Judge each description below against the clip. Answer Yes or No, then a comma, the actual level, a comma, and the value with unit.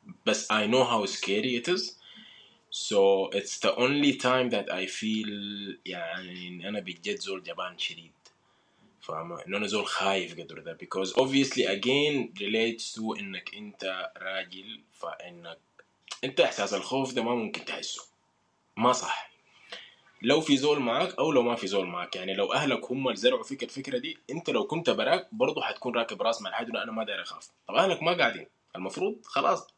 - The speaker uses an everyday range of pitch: No, wide, 7.1 semitones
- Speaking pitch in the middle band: No, low, 120 Hz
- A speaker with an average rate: Yes, average, 170 wpm